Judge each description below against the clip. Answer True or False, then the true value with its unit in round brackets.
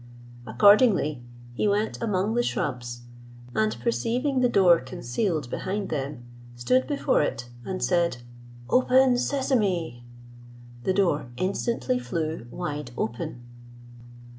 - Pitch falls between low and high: True (175 Hz)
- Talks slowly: True (110 wpm)